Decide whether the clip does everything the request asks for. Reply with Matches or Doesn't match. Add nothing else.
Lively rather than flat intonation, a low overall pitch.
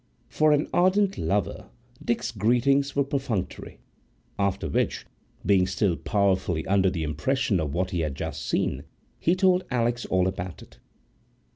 Matches